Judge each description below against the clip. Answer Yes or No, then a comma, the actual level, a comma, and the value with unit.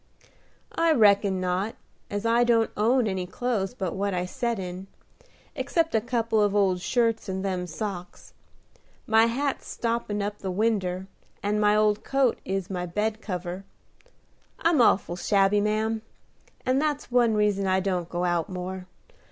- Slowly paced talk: No, average, 155 wpm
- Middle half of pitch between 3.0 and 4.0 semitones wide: Yes, average, 3.5 semitones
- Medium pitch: No, high, 205 Hz